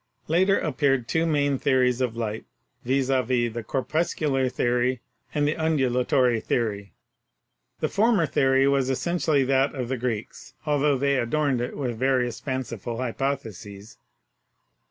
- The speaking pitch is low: Yes, low, 130 Hz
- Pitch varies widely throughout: No, average, 2.9 semitones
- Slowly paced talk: Yes, slow, 130 wpm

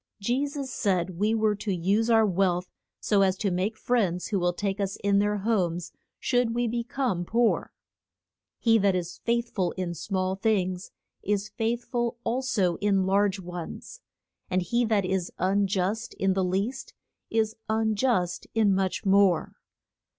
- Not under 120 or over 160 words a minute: No, average, 170 wpm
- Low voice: No, high, 200 Hz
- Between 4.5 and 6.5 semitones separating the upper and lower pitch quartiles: No, average, 3.4 semitones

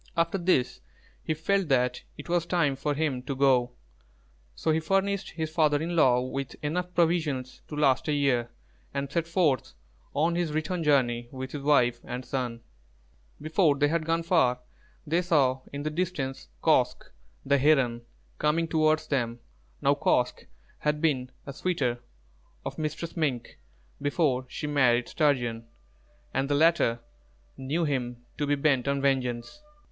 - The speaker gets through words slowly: No, average, 155 wpm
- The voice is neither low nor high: Yes, medium, 145 Hz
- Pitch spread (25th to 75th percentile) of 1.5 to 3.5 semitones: No, average, 3.9 semitones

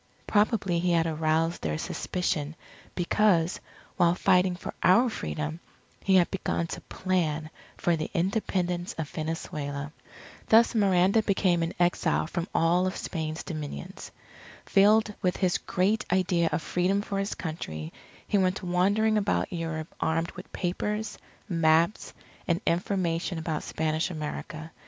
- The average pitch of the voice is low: No, medium, 175 Hz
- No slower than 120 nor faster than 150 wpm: Yes, slow, 135 wpm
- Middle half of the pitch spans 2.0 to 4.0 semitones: Yes, average, 3.0 semitones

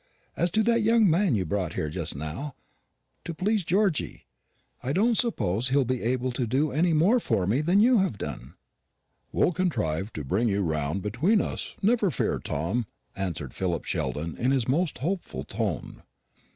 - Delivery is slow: No, average, 175 wpm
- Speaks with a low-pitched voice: Yes, low, 130 Hz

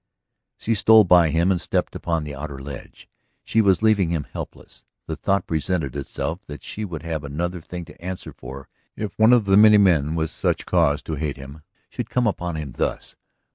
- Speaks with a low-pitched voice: Yes, very low, 85 Hz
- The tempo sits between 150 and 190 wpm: No, average, 200 wpm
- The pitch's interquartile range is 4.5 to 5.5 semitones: Yes, average, 4.8 semitones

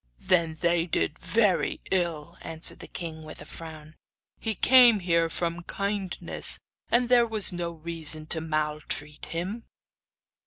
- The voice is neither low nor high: Yes, medium, 170 Hz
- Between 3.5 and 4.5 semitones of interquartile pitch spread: Yes, average, 3.8 semitones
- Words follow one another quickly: No, average, 140 wpm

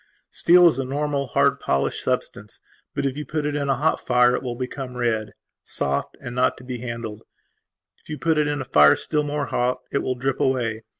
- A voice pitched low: Yes, low, 130 Hz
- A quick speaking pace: Yes, fast, 220 wpm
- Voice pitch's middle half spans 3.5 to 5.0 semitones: No, average, 3.1 semitones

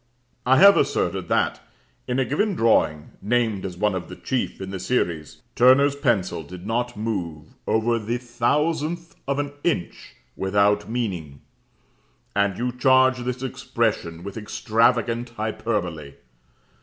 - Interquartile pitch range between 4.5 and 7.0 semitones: Yes, average, 4.9 semitones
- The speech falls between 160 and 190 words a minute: No, slow, 135 wpm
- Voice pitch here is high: No, low, 115 Hz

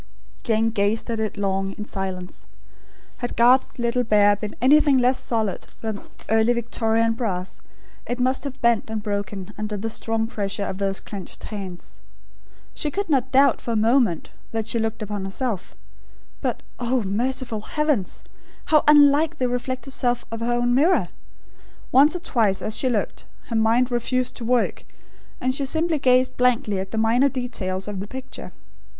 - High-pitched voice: Yes, high, 230 Hz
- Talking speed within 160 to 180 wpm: Yes, average, 170 wpm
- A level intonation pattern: No, average, 3.6 semitones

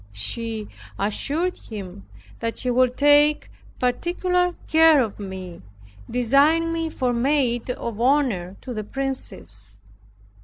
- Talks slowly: Yes, slow, 115 wpm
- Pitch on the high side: Yes, very high, 250 Hz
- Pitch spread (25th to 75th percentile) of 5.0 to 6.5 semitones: Yes, average, 5.3 semitones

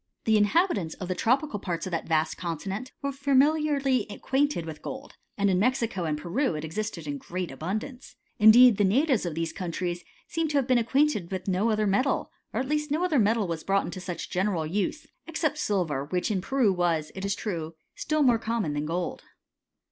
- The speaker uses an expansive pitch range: Yes, wide, 7.2 semitones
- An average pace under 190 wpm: No, average, 200 wpm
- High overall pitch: Yes, high, 205 Hz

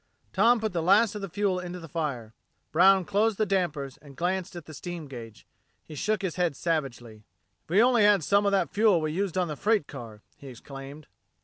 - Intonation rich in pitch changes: Yes, wide, 5.7 semitones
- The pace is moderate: No, fast, 215 wpm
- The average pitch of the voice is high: No, medium, 175 Hz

